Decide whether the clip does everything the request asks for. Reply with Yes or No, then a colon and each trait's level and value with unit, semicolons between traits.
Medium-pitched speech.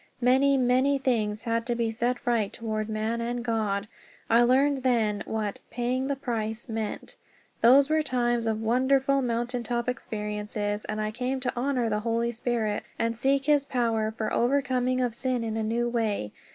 No: high, 235 Hz